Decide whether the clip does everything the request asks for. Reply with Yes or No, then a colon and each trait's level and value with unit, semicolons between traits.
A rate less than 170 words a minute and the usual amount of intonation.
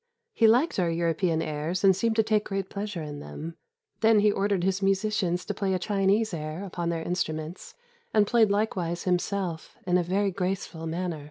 No: average, 185 wpm; average, 3.2 semitones